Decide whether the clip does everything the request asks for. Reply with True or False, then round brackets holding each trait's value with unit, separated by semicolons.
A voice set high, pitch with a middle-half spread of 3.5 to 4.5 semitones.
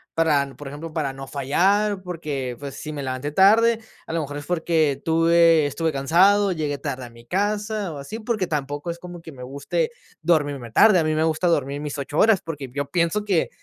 False (160 Hz; 4.2 semitones)